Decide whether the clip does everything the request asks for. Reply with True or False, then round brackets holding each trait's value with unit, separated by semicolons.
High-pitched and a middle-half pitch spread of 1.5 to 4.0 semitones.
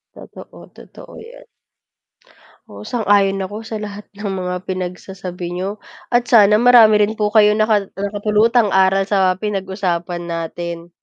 True (200 Hz; 2.5 semitones)